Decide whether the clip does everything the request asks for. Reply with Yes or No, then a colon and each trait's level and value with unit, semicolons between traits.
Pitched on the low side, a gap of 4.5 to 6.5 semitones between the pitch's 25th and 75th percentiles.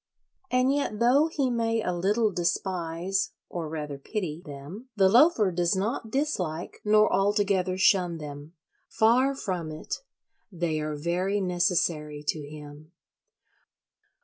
No: medium, 185 Hz; average, 5.2 semitones